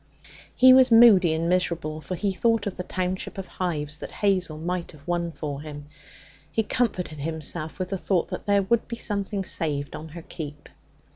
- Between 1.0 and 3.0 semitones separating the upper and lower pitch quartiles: No, average, 4.3 semitones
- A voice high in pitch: No, medium, 180 Hz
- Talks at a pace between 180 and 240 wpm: Yes, average, 190 wpm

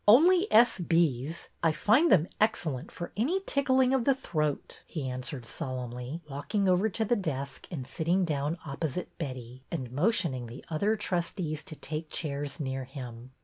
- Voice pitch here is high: No, medium, 160 Hz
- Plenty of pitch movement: Yes, wide, 7.1 semitones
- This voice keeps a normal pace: Yes, average, 160 wpm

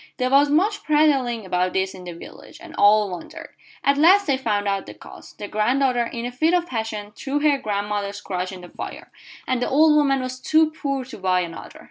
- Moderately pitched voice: No, high, 245 Hz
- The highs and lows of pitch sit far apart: Yes, wide, 6.0 semitones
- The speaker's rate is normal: No, fast, 215 wpm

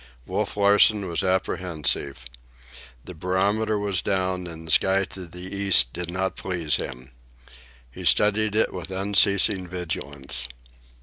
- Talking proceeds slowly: Yes, slow, 130 wpm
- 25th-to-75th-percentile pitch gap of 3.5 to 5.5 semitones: No, average, 2.9 semitones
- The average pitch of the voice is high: No, very low, 95 Hz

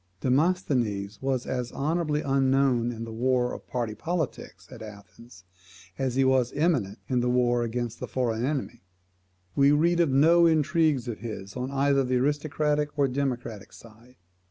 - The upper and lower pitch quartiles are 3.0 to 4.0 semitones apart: Yes, average, 3.5 semitones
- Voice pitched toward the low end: Yes, low, 130 Hz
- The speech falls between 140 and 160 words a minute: Yes, average, 155 wpm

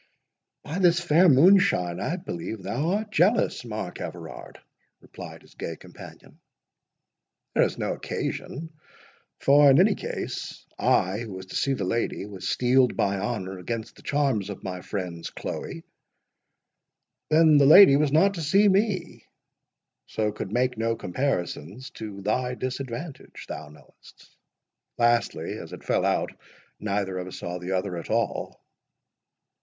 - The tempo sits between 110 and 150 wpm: Yes, average, 140 wpm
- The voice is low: Yes, low, 120 Hz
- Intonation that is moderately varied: No, wide, 8.1 semitones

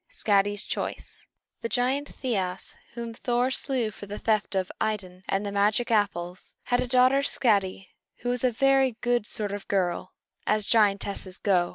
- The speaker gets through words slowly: No, average, 165 wpm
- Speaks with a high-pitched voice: Yes, high, 215 Hz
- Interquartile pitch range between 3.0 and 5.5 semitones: Yes, average, 3.7 semitones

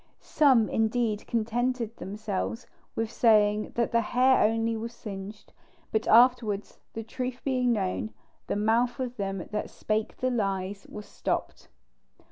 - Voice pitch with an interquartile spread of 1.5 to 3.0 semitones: Yes, narrow, 2.5 semitones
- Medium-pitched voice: No, high, 225 Hz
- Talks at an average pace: No, slow, 130 wpm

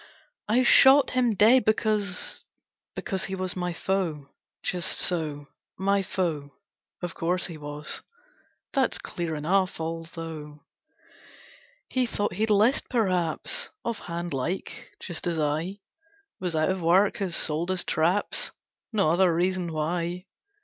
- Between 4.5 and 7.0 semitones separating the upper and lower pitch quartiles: No, average, 3.5 semitones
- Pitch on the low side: No, medium, 180 Hz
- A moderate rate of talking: No, slow, 130 wpm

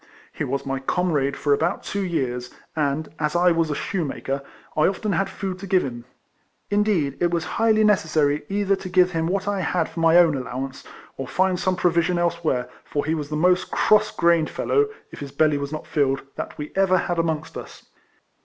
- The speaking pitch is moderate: Yes, medium, 165 Hz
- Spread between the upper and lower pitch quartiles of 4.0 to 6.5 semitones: Yes, average, 4.3 semitones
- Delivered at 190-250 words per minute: Yes, average, 200 wpm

